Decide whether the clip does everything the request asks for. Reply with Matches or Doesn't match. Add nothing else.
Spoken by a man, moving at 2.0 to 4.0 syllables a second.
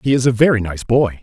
Doesn't match